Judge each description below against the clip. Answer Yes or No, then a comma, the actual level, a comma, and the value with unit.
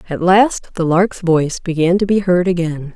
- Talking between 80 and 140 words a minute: No, fast, 205 wpm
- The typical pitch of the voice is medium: Yes, medium, 175 Hz